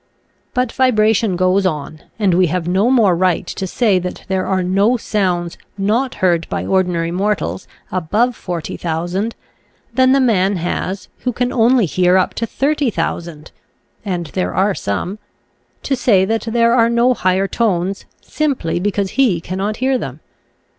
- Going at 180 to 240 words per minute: No, average, 155 wpm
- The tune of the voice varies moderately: Yes, average, 4.5 semitones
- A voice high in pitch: Yes, high, 195 Hz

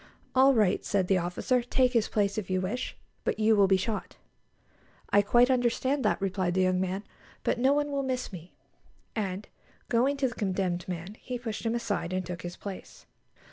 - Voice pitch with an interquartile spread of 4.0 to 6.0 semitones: Yes, average, 4.9 semitones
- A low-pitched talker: No, high, 205 Hz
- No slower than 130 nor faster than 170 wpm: No, average, 200 wpm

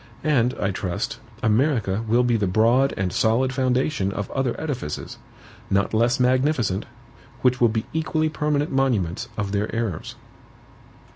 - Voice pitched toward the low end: Yes, low, 120 Hz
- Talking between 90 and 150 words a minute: Yes, average, 140 wpm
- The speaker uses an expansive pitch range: No, average, 4.4 semitones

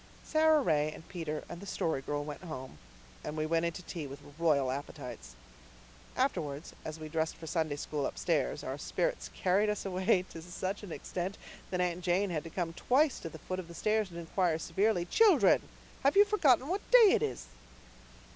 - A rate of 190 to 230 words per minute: Yes, average, 195 wpm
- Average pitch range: Yes, average, 4.7 semitones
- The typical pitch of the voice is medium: Yes, medium, 170 Hz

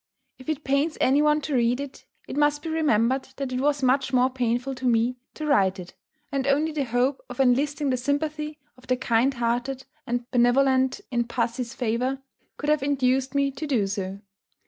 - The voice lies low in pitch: No, very high, 260 Hz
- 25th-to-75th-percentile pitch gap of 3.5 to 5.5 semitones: No, average, 2.7 semitones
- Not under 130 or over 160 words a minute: No, average, 190 wpm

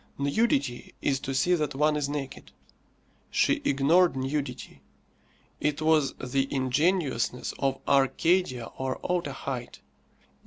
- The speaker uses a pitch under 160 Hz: Yes, medium, 140 Hz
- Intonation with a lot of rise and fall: No, narrow, 2.5 semitones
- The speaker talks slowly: Yes, slow, 110 wpm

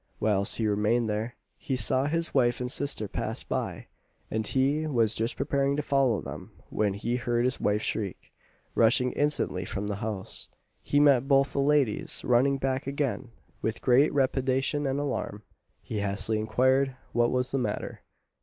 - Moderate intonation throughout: Yes, average, 3.9 semitones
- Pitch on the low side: Yes, low, 125 Hz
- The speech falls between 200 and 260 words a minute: No, average, 165 wpm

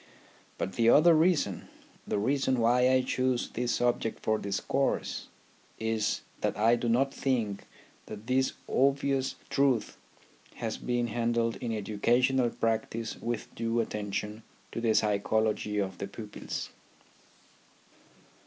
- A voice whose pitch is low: Yes, low, 115 Hz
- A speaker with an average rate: No, slow, 125 wpm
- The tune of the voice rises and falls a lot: No, average, 3.1 semitones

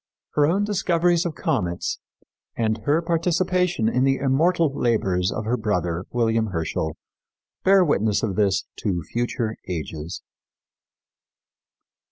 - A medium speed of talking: No, slow, 120 wpm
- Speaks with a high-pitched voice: No, low, 115 Hz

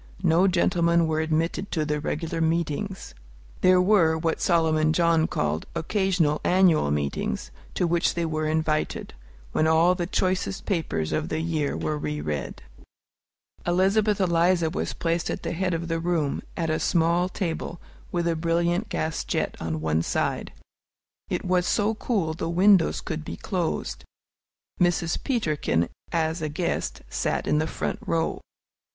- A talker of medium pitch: Yes, medium, 165 Hz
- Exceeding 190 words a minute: No, average, 155 wpm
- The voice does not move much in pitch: Yes, narrow, 2.3 semitones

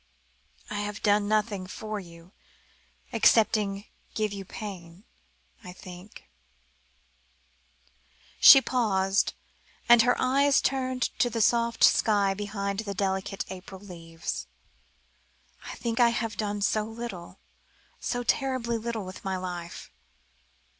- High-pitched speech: Yes, high, 205 Hz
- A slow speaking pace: Yes, slow, 120 wpm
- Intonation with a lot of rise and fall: No, average, 3.6 semitones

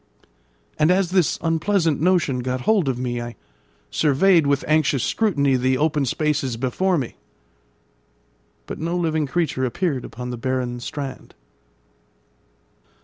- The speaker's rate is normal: No, slow, 130 wpm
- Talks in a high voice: No, medium, 145 Hz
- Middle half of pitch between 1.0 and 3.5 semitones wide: No, average, 4.7 semitones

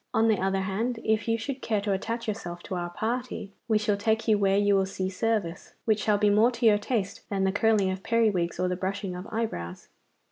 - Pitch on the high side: Yes, high, 205 Hz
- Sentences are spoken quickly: Yes, fast, 235 wpm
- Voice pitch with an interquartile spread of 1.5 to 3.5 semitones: Yes, average, 2.8 semitones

